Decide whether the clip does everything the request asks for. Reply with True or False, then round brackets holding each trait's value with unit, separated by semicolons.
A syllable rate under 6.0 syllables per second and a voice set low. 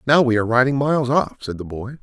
False (6.7 syllables/s; 125 Hz)